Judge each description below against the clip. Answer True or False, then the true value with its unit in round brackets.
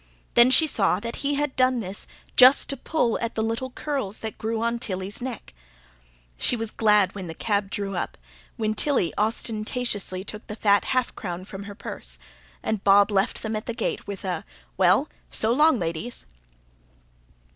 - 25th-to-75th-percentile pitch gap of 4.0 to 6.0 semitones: False (3.5 semitones)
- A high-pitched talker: True (220 Hz)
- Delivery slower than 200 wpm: True (180 wpm)